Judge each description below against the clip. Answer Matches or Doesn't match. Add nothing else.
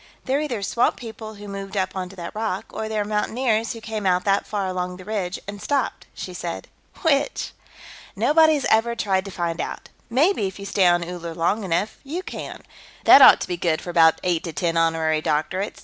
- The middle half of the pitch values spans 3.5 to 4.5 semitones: Matches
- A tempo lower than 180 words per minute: Doesn't match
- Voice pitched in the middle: Doesn't match